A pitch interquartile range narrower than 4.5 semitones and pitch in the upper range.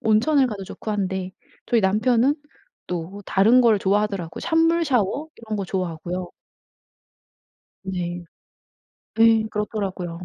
Yes: average, 3.5 semitones; high, 205 Hz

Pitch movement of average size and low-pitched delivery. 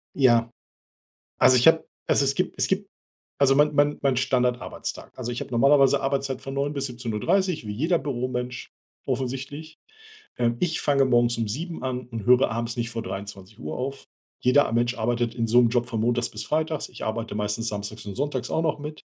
Yes: average, 3.2 semitones; low, 125 Hz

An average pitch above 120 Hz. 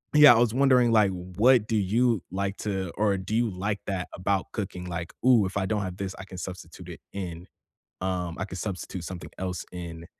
No: very low, 95 Hz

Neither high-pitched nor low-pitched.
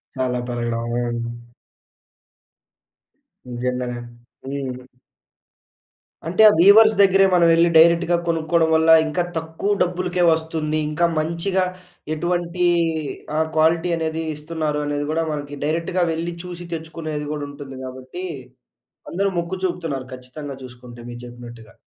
Yes: medium, 160 Hz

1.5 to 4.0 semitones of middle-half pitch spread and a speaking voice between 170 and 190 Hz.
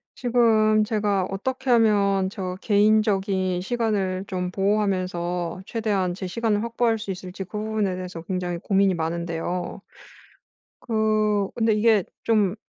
No: average, 2.9 semitones; high, 200 Hz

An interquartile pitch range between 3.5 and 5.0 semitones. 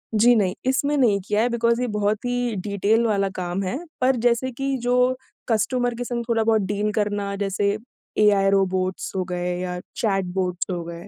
Yes: average, 4.0 semitones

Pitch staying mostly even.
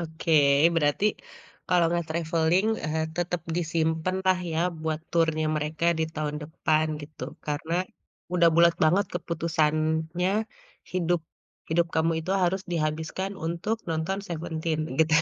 Yes: narrow, 1.6 semitones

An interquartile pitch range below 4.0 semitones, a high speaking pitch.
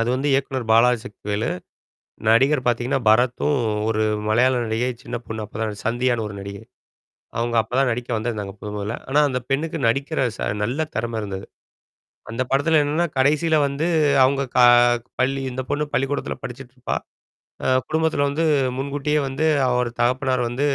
No: average, 3.4 semitones; low, 125 Hz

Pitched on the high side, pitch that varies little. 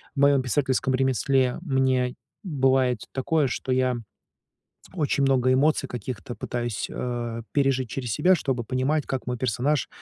No: low, 130 Hz; narrow, 1.8 semitones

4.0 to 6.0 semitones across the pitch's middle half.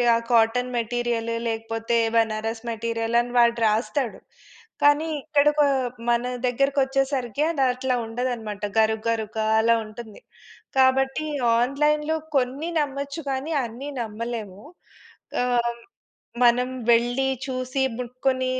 No: average, 2.9 semitones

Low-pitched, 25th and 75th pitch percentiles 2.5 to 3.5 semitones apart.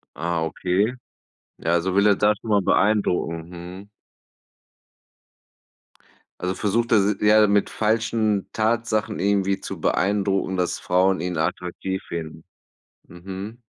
Yes: low, 100 Hz; average, 2.8 semitones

